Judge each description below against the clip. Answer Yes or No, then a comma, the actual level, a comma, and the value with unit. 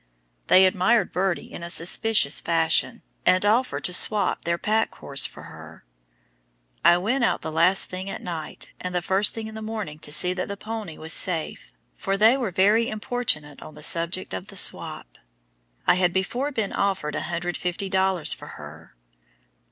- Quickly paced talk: No, average, 175 wpm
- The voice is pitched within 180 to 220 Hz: Yes, medium, 185 Hz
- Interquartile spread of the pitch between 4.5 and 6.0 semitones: No, average, 4.1 semitones